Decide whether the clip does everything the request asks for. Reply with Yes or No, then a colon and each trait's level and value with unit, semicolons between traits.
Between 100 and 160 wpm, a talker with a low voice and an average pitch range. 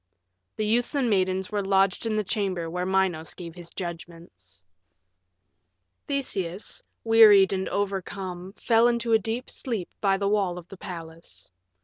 No: average, 150 wpm; high, 190 Hz; average, 3.4 semitones